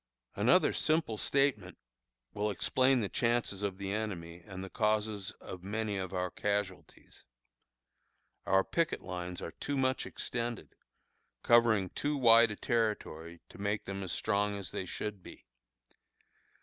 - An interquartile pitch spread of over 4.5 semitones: No, average, 3.6 semitones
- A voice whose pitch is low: Yes, low, 105 Hz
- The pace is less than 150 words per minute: Yes, average, 140 wpm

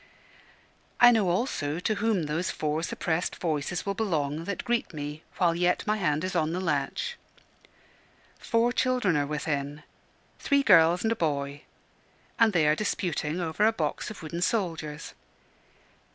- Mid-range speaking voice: Yes, medium, 170 Hz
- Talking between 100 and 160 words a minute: Yes, average, 150 wpm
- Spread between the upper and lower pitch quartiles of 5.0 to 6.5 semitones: Yes, wide, 5.6 semitones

